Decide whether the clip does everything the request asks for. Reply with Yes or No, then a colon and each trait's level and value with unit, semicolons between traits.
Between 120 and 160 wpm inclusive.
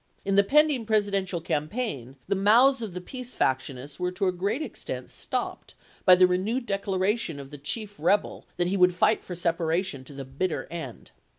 No: average, 195 wpm